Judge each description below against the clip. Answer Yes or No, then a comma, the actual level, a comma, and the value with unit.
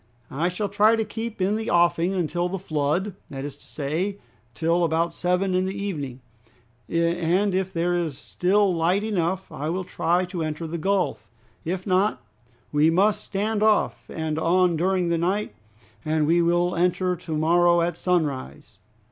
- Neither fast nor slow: Yes, average, 170 wpm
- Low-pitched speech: No, medium, 175 Hz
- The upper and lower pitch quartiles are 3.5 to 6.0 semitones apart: No, average, 2.7 semitones